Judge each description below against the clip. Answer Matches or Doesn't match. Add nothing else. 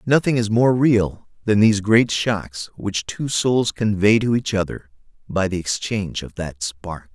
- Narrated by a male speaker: Matches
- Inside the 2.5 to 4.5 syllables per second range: Matches